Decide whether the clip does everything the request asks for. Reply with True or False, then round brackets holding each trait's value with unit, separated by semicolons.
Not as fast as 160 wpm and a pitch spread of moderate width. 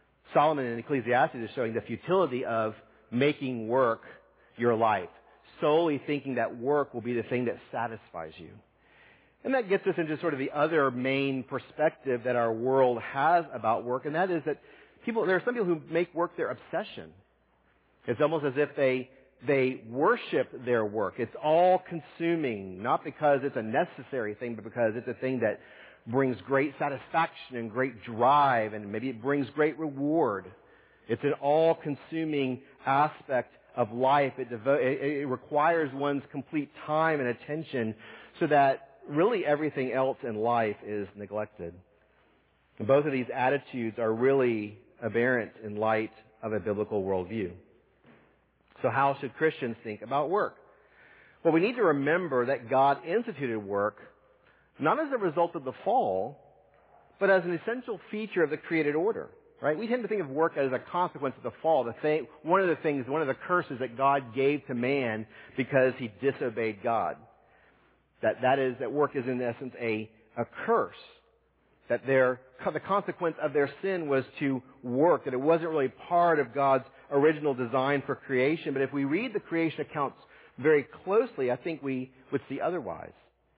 False (170 wpm; 4.0 semitones)